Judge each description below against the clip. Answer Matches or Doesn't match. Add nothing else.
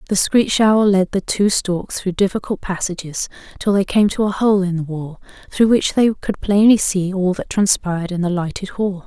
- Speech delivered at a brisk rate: Matches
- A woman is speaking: Matches